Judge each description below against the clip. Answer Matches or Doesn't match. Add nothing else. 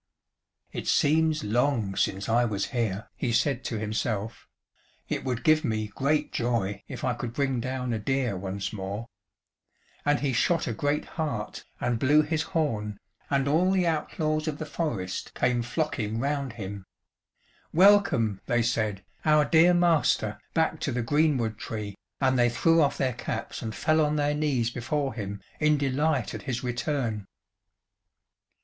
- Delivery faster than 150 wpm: Matches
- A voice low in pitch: Matches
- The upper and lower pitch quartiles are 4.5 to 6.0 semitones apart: Matches